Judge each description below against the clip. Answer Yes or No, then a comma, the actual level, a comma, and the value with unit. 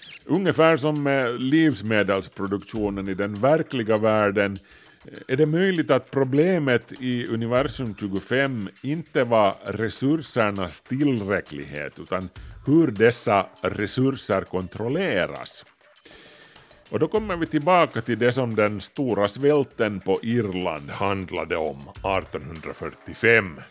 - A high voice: No, low, 115 Hz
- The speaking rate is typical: No, slow, 105 wpm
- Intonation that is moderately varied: No, wide, 5.8 semitones